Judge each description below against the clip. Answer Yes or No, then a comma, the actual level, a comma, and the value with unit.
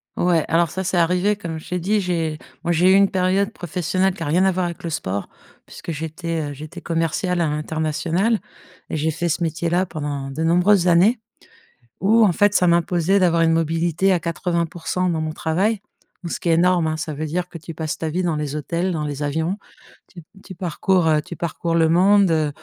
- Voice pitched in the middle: Yes, medium, 170 Hz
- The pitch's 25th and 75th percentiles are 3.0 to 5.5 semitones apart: No, narrow, 2.4 semitones